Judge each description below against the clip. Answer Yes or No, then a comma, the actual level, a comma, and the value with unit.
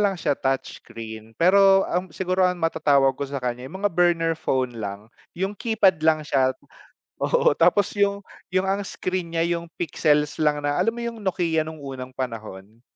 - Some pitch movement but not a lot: No, wide, 6.2 semitones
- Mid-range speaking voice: Yes, medium, 165 Hz